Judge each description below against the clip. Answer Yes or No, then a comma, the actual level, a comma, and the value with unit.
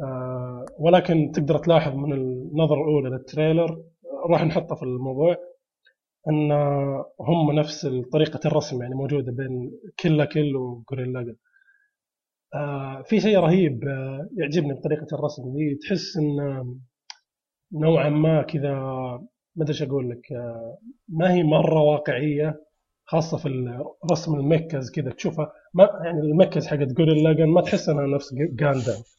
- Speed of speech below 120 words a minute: No, average, 125 wpm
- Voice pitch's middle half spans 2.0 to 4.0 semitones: Yes, average, 3.2 semitones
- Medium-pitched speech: Yes, medium, 150 Hz